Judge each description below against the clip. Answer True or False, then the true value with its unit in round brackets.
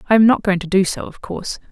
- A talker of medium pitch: False (195 Hz)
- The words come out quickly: True (315 wpm)